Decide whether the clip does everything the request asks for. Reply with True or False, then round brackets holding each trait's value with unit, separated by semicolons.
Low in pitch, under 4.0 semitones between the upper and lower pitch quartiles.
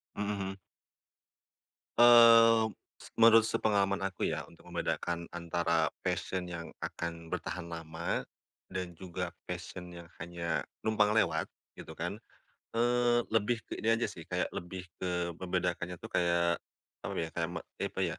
False (90 Hz; 4.3 semitones)